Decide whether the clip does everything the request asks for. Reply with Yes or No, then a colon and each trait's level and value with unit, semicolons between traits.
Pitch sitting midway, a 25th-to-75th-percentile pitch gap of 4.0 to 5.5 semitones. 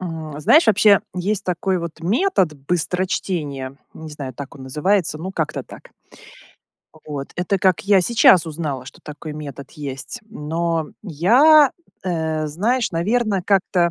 Yes: medium, 170 Hz; average, 4.4 semitones